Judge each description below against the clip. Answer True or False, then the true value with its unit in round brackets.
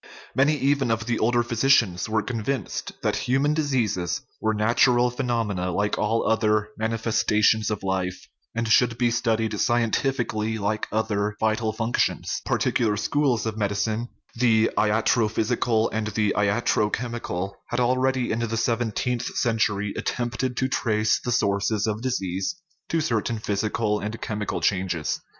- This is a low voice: True (110 Hz)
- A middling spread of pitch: False (2.3 semitones)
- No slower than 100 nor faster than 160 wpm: True (140 wpm)